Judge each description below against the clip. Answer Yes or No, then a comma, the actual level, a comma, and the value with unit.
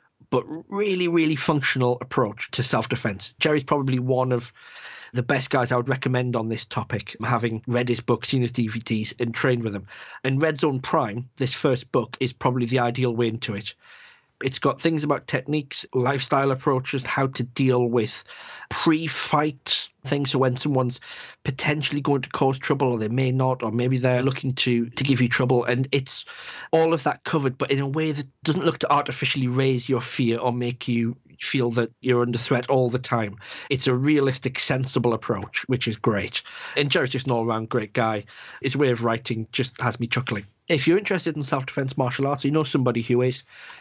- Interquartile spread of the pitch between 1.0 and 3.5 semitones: Yes, narrow, 2.6 semitones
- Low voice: Yes, low, 130 Hz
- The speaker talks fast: No, average, 195 wpm